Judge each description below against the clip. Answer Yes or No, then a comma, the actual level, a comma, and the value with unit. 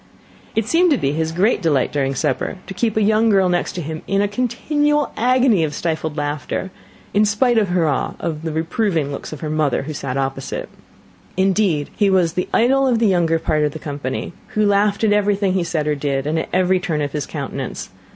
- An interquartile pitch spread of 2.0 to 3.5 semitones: No, wide, 5.6 semitones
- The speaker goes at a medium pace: No, fast, 215 wpm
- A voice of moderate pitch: Yes, medium, 180 Hz